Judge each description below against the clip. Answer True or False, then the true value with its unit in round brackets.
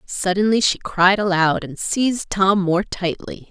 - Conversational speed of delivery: True (155 wpm)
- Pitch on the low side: False (190 Hz)